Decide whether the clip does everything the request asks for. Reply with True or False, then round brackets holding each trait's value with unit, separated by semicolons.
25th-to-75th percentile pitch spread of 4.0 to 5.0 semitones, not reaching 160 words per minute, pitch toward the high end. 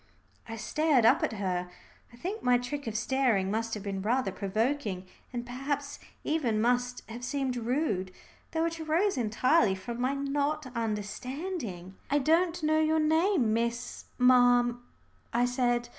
True (4.6 semitones; 150 wpm; 245 Hz)